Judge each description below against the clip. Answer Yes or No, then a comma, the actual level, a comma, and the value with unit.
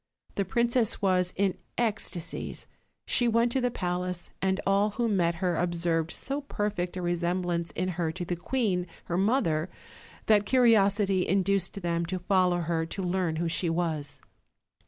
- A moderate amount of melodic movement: Yes, average, 3.0 semitones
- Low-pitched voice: No, medium, 185 Hz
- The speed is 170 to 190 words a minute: No, average, 160 wpm